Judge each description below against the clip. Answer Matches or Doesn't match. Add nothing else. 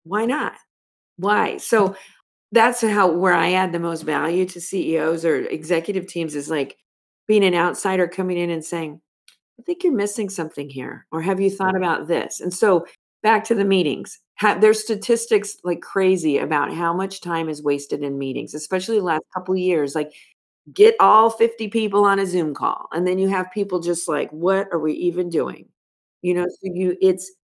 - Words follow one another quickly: Doesn't match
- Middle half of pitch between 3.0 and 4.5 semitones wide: Matches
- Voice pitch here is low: Doesn't match